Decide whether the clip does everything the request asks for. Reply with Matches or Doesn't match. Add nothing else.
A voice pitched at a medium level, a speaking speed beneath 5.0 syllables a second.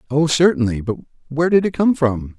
Doesn't match